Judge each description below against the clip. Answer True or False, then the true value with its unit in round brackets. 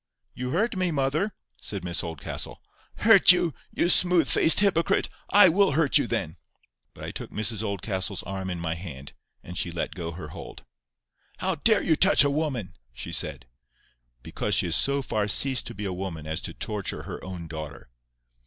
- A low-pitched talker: True (105 Hz)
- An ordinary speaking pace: True (185 wpm)